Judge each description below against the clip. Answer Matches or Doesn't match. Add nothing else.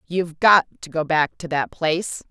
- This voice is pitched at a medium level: Matches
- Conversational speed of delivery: Doesn't match